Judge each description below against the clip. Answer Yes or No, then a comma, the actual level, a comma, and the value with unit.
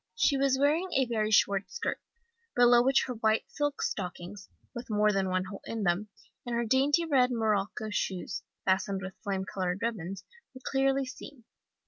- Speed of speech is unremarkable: Yes, average, 170 wpm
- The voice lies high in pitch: Yes, high, 220 Hz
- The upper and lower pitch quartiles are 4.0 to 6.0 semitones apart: Yes, average, 5.3 semitones